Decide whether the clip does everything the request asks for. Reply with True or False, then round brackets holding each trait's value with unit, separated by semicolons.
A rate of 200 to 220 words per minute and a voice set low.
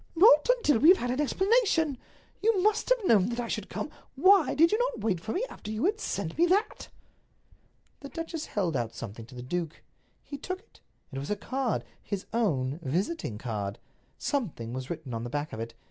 False (205 wpm; 235 Hz)